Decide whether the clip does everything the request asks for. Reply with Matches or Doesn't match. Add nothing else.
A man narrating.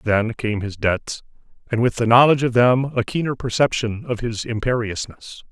Matches